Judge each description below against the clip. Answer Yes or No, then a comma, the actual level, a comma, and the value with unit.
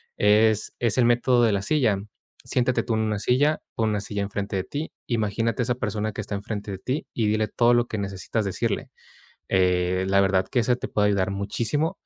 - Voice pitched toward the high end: No, low, 110 Hz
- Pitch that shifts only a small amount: No, average, 3.2 semitones